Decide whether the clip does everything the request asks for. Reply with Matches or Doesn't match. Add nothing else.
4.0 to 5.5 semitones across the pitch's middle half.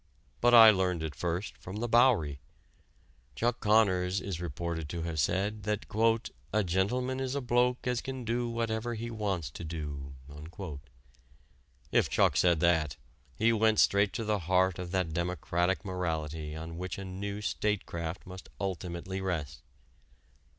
Matches